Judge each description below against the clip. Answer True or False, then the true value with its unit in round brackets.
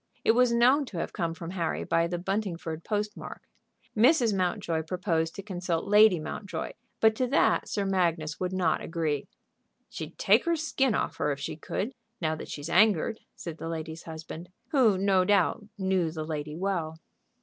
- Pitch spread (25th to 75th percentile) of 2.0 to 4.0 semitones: False (4.4 semitones)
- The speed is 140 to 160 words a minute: False (180 wpm)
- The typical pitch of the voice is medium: True (180 Hz)